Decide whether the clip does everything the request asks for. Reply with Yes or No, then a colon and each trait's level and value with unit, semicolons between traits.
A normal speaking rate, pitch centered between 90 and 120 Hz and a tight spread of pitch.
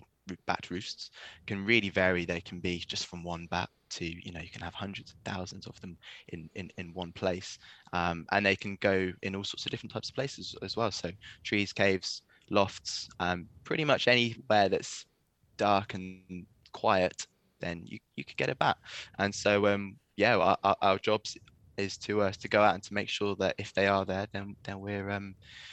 No: fast, 210 wpm; very low, 95 Hz; narrow, 2.0 semitones